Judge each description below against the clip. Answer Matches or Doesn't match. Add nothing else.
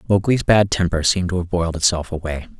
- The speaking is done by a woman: Doesn't match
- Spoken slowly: Doesn't match